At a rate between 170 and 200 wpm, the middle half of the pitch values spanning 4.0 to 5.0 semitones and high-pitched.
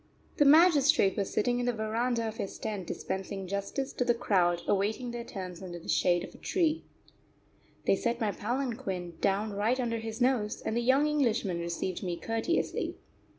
Yes: average, 180 wpm; average, 4.3 semitones; high, 220 Hz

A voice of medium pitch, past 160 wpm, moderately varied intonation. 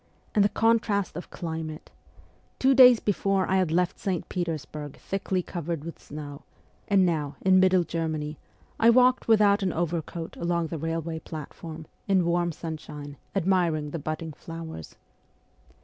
No: medium, 170 Hz; average, 145 wpm; average, 3.2 semitones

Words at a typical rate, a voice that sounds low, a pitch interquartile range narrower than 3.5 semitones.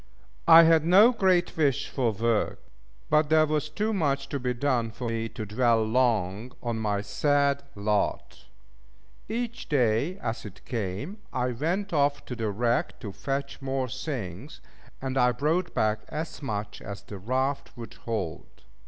No: average, 160 wpm; low, 130 Hz; wide, 5.4 semitones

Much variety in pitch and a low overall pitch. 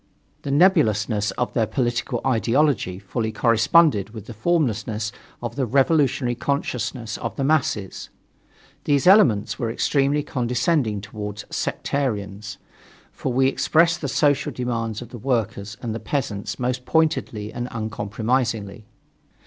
No: average, 4.5 semitones; low, 120 Hz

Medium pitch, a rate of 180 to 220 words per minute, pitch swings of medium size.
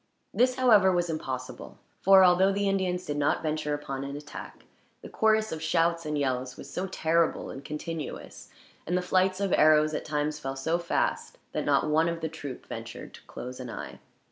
Yes: medium, 160 Hz; average, 195 wpm; average, 3.8 semitones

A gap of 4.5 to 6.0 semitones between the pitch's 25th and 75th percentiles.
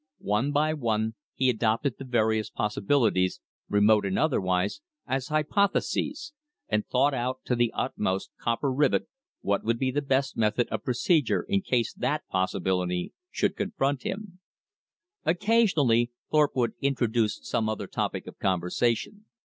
Yes: average, 5.2 semitones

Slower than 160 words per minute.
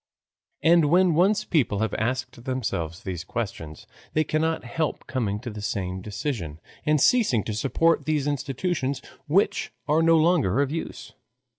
Yes: average, 150 wpm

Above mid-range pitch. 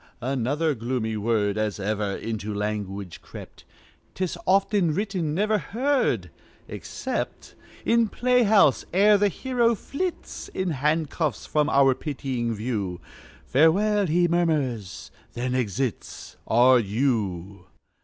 No: low, 135 Hz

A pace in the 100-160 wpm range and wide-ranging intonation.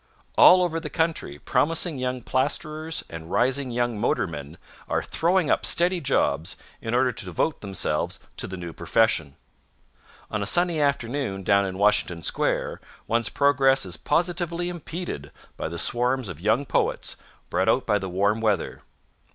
Yes: average, 155 wpm; wide, 8.3 semitones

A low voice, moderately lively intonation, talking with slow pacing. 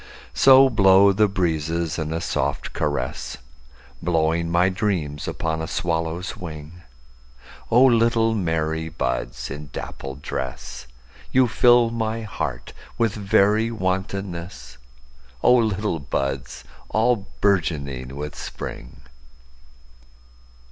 No: very low, 80 Hz; wide, 7.4 semitones; slow, 95 wpm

